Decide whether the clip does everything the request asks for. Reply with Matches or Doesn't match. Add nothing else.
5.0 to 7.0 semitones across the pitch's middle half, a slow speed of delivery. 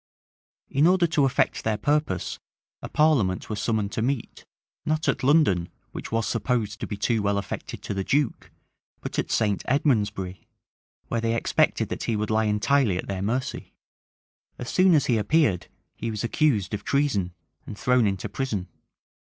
Doesn't match